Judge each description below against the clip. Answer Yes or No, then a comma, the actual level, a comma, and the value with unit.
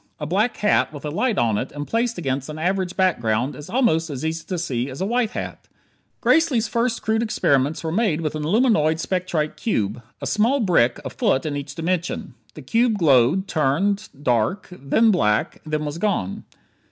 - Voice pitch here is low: No, medium, 165 Hz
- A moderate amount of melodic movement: No, wide, 6.8 semitones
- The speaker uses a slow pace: No, average, 190 wpm